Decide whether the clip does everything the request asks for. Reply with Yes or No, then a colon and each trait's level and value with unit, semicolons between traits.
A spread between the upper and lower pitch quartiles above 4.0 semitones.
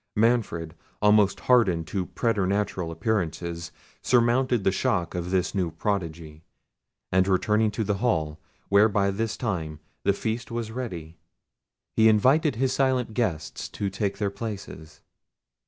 Yes: average, 4.5 semitones